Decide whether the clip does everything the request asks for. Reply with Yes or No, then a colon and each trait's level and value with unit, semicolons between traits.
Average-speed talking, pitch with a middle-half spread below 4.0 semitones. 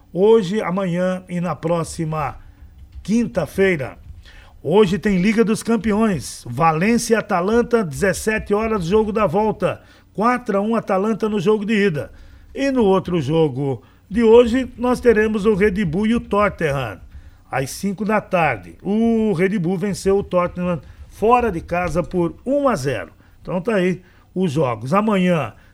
No: average, 150 wpm; average, 5.1 semitones